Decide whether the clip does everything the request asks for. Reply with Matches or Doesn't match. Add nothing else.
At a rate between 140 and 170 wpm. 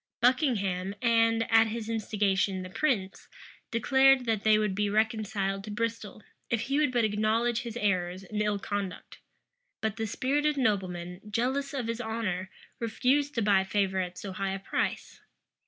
Matches